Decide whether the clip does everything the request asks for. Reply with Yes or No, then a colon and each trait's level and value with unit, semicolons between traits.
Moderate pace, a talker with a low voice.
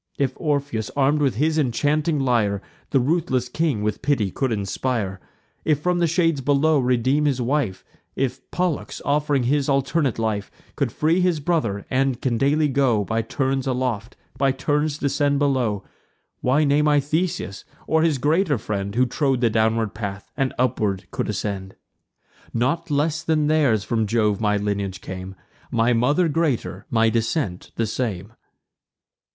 Yes: average, 155 wpm; low, 130 Hz